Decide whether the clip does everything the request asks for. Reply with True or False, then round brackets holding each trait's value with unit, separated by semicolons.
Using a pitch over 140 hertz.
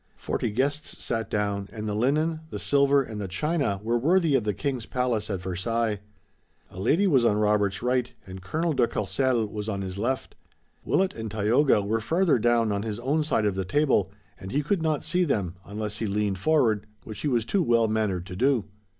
False (115 Hz)